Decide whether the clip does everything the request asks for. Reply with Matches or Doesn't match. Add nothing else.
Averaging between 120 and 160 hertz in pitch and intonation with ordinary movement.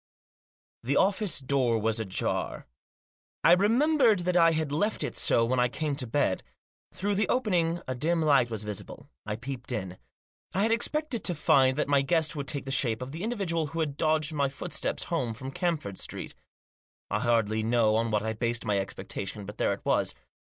Doesn't match